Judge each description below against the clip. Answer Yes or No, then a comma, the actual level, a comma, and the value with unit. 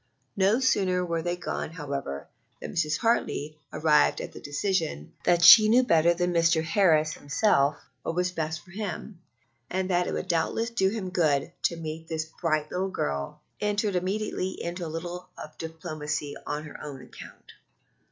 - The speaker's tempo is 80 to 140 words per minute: No, average, 170 wpm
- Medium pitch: Yes, medium, 170 Hz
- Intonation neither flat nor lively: Yes, average, 3.3 semitones